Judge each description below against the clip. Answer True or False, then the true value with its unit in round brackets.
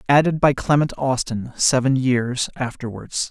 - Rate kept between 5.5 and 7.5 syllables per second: False (4.4 syllables/s)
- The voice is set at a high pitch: False (130 Hz)